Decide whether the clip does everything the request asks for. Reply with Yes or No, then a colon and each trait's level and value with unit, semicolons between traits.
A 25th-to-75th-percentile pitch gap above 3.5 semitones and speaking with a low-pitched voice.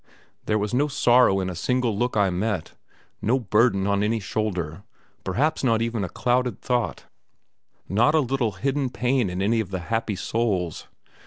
Yes: average, 4.2 semitones; low, 110 Hz